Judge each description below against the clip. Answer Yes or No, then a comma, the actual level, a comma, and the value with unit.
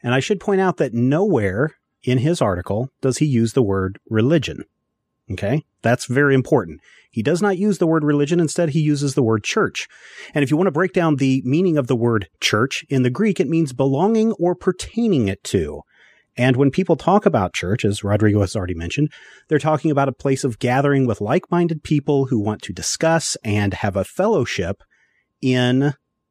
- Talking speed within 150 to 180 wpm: No, average, 195 wpm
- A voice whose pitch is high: No, medium, 140 Hz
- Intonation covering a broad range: Yes, wide, 5.9 semitones